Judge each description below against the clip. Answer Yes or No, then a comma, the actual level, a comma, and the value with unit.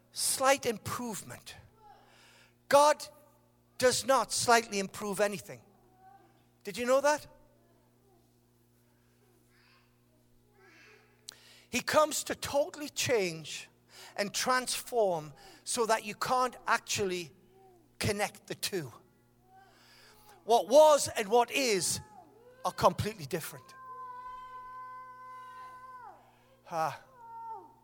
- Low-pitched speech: No, high, 245 Hz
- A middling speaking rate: No, slow, 80 wpm